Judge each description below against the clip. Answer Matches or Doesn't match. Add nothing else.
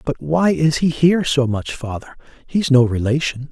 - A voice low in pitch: Doesn't match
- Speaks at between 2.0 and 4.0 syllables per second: Doesn't match